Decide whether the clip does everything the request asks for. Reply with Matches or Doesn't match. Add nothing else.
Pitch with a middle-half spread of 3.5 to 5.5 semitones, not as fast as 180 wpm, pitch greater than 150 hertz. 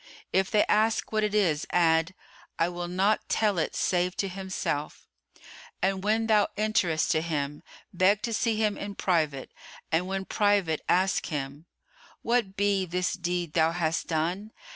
Matches